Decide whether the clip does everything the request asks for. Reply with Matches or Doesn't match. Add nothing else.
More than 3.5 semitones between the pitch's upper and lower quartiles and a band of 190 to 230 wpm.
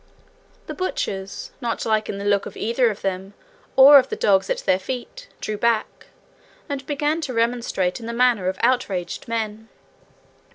Doesn't match